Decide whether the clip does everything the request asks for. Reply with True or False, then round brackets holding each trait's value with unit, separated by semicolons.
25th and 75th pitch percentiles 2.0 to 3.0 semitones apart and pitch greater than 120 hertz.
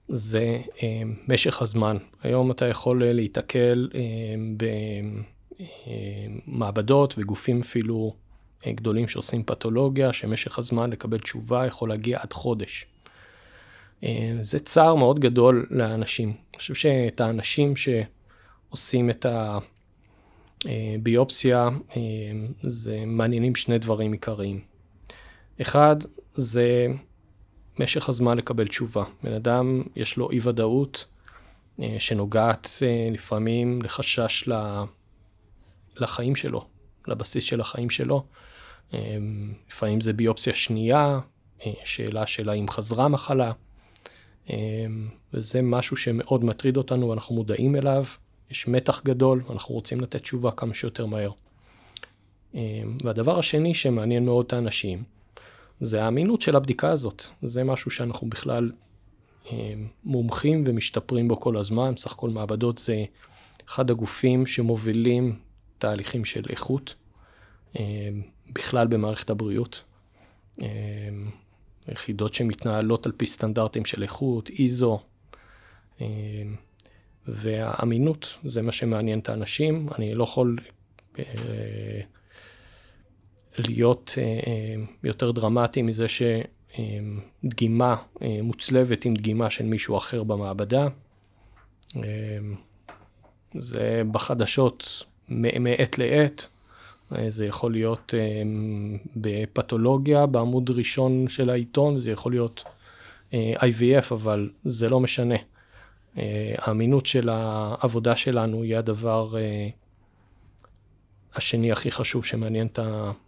False (2.7 semitones; 115 Hz)